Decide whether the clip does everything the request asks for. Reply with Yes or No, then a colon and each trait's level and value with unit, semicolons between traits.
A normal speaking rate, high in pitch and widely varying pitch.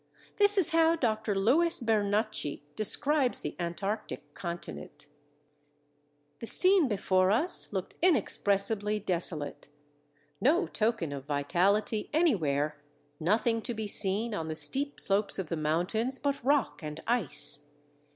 No: slow, 120 wpm; high, 210 Hz; wide, 7.0 semitones